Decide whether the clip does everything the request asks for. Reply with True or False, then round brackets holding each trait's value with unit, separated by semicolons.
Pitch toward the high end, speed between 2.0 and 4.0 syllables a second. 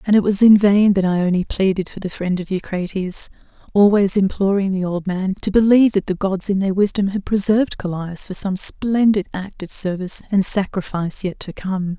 False (195 Hz; 5.2 syllables/s)